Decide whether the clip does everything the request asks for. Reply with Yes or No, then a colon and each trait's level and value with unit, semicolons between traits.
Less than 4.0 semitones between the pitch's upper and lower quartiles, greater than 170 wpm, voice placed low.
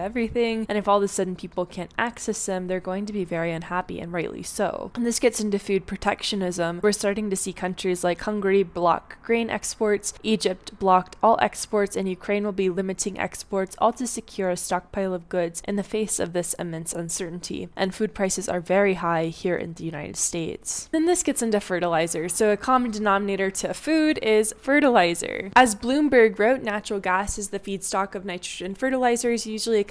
No: average, 3.0 semitones; average, 195 wpm; high, 200 Hz